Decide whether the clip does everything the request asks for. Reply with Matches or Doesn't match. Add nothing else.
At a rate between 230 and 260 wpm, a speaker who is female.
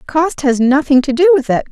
Matches